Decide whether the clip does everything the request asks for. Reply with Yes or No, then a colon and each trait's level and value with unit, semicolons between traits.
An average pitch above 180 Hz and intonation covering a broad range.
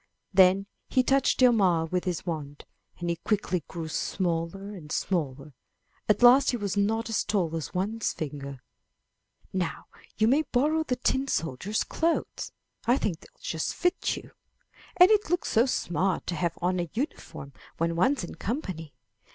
Yes: high, 190 Hz; wide, 6.7 semitones